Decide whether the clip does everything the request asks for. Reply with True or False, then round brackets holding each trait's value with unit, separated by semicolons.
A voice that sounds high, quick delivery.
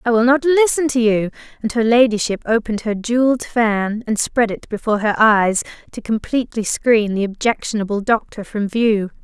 False (225 Hz; 175 wpm)